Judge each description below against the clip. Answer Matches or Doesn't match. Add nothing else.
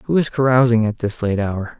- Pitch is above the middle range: Doesn't match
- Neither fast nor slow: Doesn't match